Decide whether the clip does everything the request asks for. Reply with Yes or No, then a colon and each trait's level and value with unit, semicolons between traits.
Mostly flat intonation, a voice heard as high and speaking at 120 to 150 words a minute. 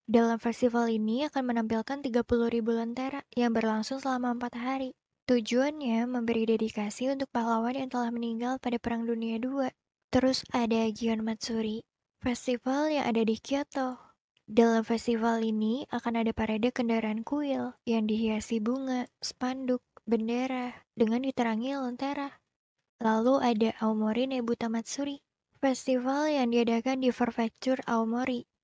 Yes: narrow, 2.1 semitones; high, 240 Hz; average, 130 wpm